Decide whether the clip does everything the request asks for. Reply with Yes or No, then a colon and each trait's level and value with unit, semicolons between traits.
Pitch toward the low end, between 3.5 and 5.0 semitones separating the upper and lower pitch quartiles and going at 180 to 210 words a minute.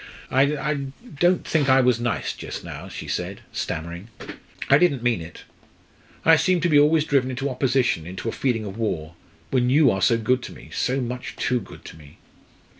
Yes: low, 125 Hz; average, 3.9 semitones; average, 190 wpm